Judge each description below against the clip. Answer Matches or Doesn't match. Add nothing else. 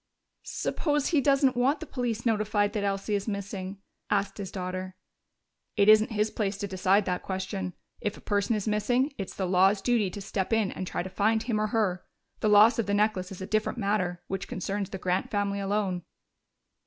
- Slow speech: Doesn't match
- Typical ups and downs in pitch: Doesn't match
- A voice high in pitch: Matches